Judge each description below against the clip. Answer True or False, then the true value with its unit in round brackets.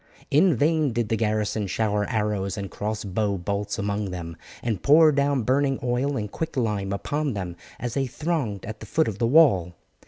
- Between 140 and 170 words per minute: False (185 wpm)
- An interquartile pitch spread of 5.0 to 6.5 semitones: True (5.5 semitones)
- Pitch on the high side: False (110 Hz)